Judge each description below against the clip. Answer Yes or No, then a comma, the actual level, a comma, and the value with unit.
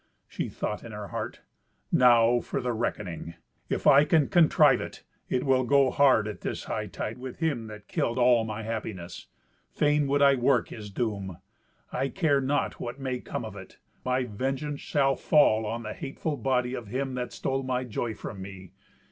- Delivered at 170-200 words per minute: Yes, average, 180 wpm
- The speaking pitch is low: Yes, low, 125 Hz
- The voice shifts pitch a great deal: No, average, 4.0 semitones